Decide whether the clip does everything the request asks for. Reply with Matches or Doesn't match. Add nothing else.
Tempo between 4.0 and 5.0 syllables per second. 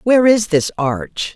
Matches